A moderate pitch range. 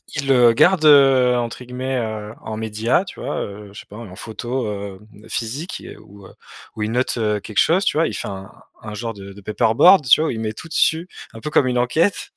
Yes: average, 4.3 semitones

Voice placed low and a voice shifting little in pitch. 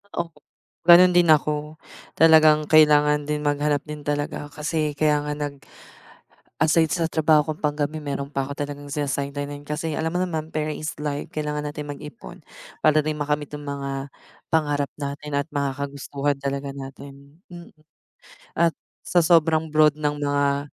No: medium, 150 Hz; narrow, 1.4 semitones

